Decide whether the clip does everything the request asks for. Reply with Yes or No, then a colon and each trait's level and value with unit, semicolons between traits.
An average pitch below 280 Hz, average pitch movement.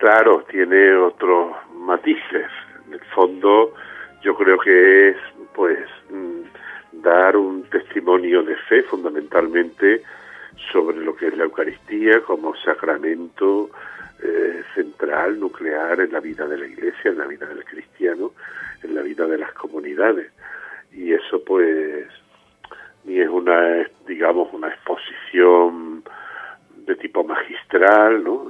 No: very high, 375 Hz; average, 4.1 semitones